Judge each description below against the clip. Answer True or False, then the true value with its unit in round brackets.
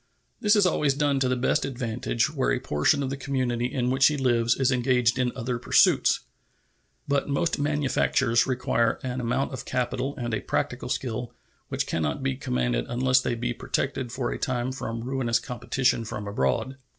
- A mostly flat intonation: True (2.2 semitones)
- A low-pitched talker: True (125 Hz)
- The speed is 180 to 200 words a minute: True (185 wpm)